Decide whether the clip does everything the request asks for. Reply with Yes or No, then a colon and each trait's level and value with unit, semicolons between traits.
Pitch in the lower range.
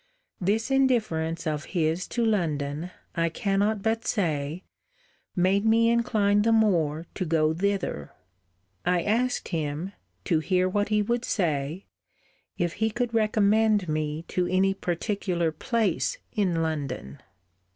No: medium, 185 Hz